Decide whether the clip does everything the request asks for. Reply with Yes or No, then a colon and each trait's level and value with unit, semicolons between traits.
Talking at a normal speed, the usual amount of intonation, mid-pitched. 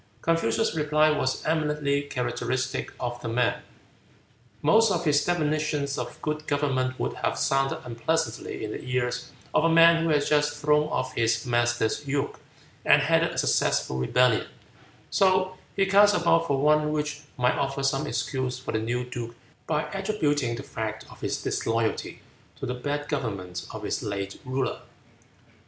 Yes: average, 160 wpm; average, 3.8 semitones; medium, 145 Hz